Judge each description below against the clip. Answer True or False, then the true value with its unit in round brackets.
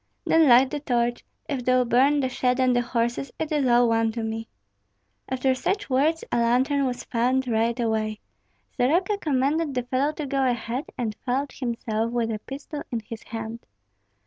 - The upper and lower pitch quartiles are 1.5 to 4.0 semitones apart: True (2.9 semitones)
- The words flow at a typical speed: True (180 wpm)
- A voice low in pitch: False (250 Hz)